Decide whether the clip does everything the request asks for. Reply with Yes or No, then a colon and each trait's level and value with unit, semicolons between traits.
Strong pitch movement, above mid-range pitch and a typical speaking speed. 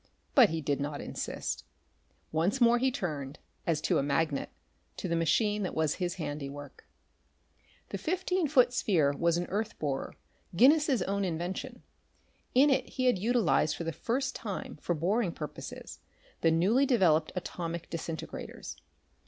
No: wide, 7.1 semitones; medium, 180 Hz; average, 150 wpm